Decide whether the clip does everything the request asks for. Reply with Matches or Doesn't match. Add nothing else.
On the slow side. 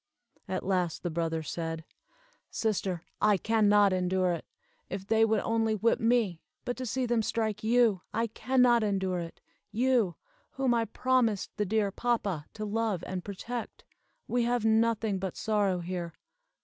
Doesn't match